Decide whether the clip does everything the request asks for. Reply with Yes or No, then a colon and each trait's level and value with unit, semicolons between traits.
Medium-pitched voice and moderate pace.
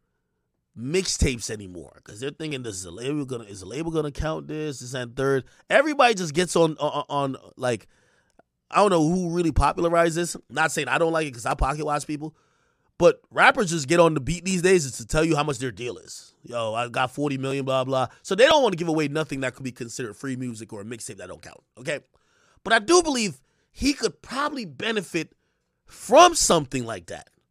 No: medium, 150 Hz; fast, 220 wpm